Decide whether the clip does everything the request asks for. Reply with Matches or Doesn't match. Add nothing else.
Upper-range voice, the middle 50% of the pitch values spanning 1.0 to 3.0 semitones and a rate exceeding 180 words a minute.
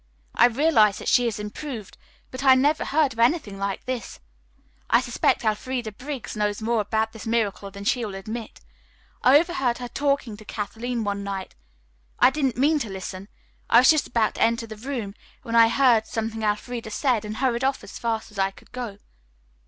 Doesn't match